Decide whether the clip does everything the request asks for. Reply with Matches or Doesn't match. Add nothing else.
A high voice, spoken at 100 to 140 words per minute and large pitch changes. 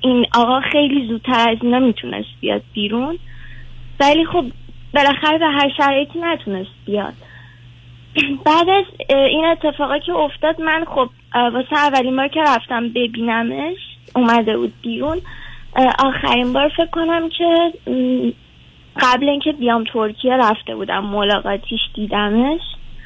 Matches